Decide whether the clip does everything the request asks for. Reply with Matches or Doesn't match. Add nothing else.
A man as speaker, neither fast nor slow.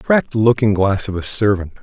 Matches